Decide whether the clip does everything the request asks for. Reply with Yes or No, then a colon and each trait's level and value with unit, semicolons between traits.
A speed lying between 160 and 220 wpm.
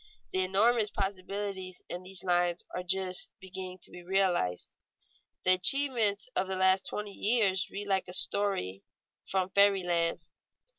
No: average, 145 wpm